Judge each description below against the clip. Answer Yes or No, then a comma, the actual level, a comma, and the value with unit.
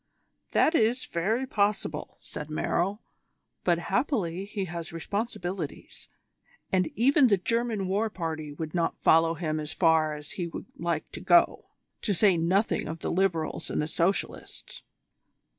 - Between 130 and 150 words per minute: Yes, average, 145 wpm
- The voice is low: No, medium, 175 Hz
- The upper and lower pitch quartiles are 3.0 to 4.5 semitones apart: Yes, average, 4.0 semitones